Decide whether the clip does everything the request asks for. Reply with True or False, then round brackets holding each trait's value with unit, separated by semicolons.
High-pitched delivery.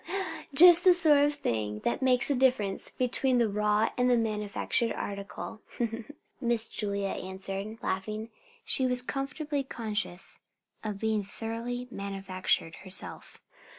True (220 Hz)